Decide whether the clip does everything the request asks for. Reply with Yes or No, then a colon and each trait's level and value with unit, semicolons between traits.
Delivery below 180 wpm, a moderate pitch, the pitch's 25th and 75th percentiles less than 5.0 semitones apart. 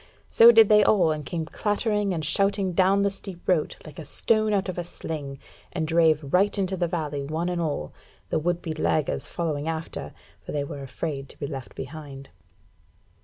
No: average, 195 wpm; medium, 165 Hz; average, 4.4 semitones